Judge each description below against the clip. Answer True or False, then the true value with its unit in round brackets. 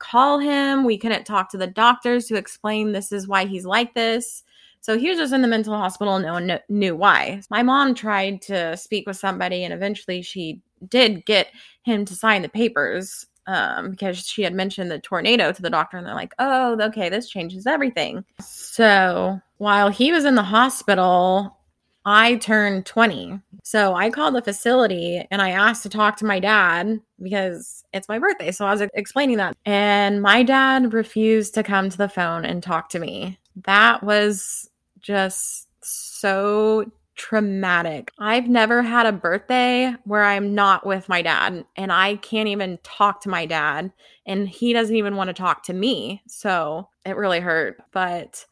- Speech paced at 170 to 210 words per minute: True (185 wpm)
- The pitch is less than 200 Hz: False (205 Hz)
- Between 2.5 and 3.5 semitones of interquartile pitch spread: True (3.0 semitones)